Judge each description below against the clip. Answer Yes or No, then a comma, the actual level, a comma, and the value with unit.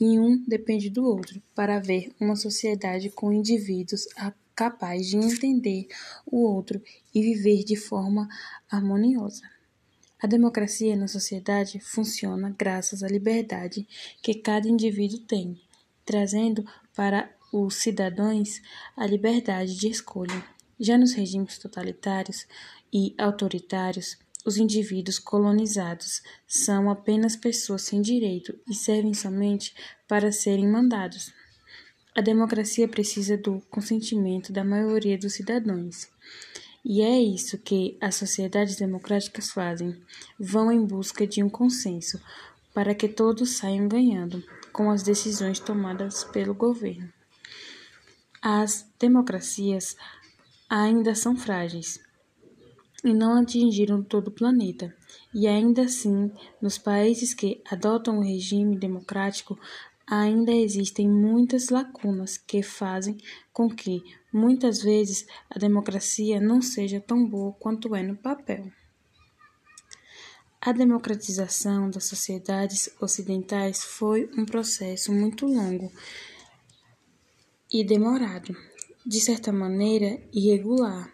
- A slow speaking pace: Yes, slow, 115 wpm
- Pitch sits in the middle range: No, high, 210 Hz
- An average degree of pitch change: No, narrow, 2.2 semitones